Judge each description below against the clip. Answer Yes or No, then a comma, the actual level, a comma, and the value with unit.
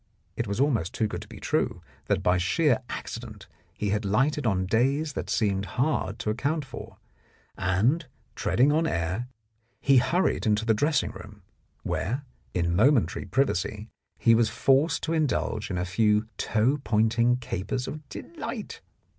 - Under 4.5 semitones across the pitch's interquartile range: No, average, 5.0 semitones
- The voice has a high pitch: No, low, 115 Hz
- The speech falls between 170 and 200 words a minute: No, average, 155 wpm